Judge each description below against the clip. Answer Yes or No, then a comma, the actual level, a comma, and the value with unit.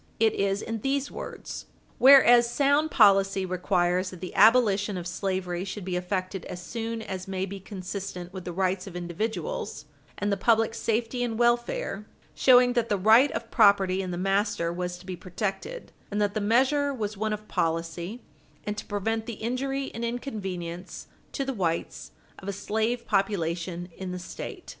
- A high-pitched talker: Yes, high, 200 Hz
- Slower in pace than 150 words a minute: No, average, 175 wpm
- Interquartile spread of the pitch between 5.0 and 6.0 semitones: No, average, 3.9 semitones